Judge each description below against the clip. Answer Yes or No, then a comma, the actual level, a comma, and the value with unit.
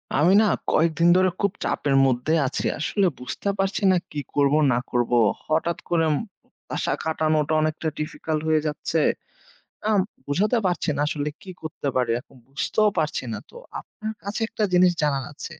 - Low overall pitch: No, medium, 155 Hz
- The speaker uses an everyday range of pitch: Yes, average, 4.1 semitones